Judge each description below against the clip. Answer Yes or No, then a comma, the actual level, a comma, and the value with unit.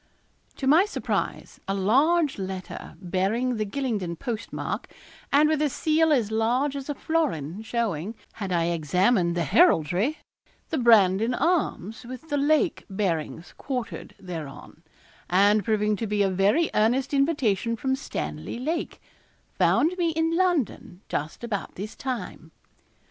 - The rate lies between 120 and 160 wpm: Yes, average, 140 wpm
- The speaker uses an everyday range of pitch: No, wide, 7.0 semitones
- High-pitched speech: Yes, high, 225 Hz